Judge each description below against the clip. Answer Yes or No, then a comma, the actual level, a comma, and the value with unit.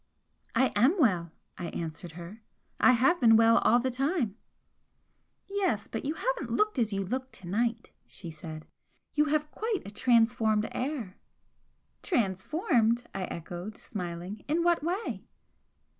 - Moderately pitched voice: No, high, 230 Hz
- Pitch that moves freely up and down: Yes, wide, 7.5 semitones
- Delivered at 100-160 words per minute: Yes, average, 145 wpm